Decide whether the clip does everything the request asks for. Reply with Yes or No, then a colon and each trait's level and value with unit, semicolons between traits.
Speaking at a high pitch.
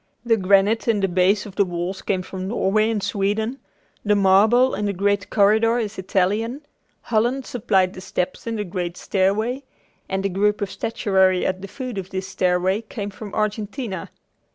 Yes: high, 200 Hz